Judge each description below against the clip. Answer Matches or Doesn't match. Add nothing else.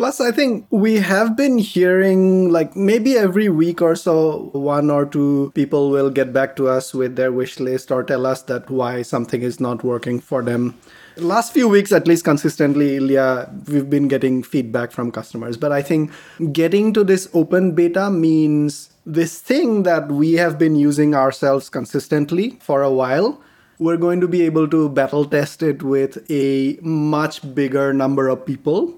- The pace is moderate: Matches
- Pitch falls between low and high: Matches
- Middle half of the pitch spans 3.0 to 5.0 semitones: Matches